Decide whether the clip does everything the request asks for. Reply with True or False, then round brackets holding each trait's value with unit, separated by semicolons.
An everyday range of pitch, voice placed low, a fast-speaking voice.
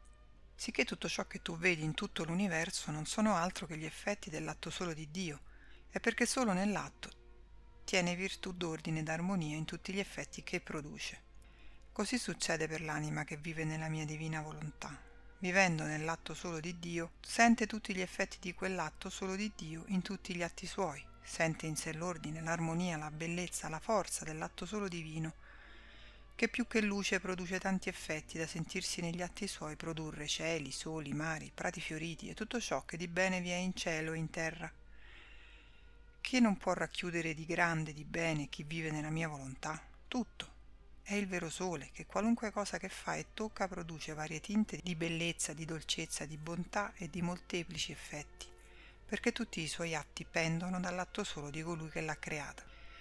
False (3.2 semitones; 170 Hz; 180 wpm)